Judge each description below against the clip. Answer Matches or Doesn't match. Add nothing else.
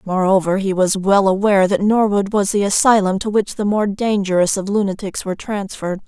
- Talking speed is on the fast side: Doesn't match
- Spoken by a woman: Matches